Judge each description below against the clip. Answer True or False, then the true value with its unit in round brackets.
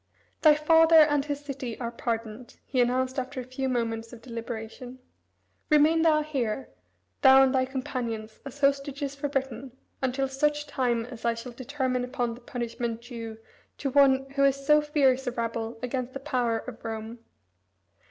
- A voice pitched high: True (260 Hz)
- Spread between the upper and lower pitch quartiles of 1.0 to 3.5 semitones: True (2.9 semitones)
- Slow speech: False (165 wpm)